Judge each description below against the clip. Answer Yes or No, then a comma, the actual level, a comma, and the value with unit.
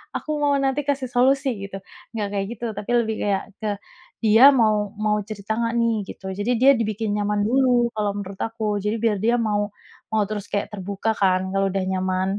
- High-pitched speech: Yes, high, 215 Hz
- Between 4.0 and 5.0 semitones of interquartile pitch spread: No, average, 2.8 semitones